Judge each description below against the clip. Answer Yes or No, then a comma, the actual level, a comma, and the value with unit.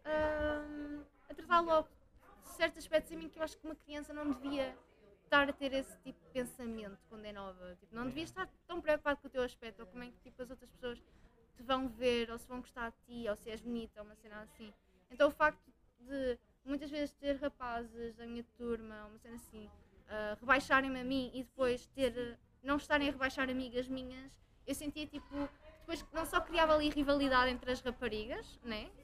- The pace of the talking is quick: Yes, fast, 215 wpm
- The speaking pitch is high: Yes, very high, 260 Hz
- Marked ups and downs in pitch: No, average, 3.8 semitones